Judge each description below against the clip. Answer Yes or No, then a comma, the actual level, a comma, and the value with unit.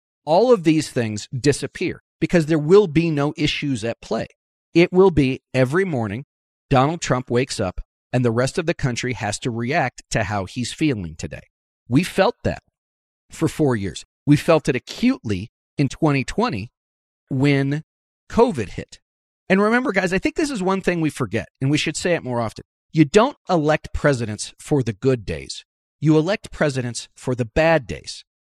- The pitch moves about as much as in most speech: No, wide, 5.8 semitones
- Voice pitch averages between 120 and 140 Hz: Yes, low, 135 Hz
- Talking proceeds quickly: No, average, 175 wpm